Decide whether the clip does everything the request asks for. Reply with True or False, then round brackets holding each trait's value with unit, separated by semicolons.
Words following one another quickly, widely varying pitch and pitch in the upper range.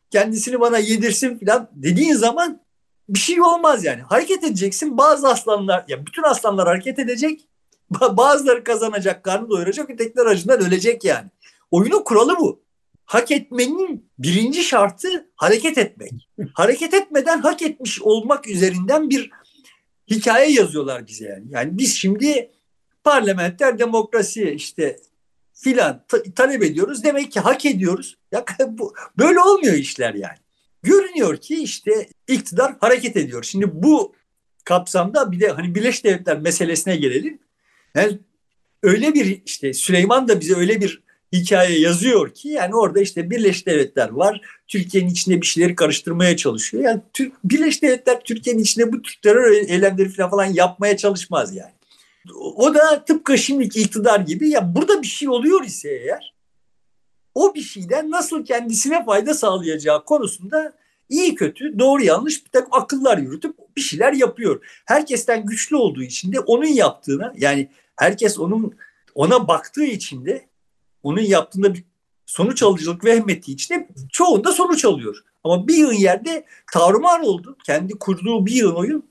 True (145 wpm; 7.6 semitones; 235 Hz)